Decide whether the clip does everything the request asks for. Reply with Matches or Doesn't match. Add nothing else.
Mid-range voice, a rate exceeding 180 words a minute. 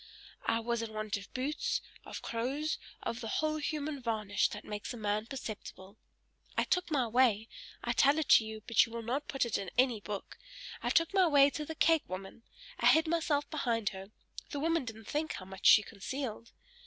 Doesn't match